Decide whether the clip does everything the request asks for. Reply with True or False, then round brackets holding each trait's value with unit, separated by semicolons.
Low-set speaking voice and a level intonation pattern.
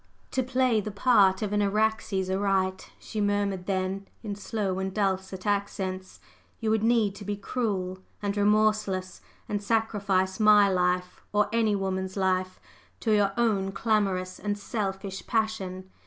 False (200 Hz; 2.1 semitones)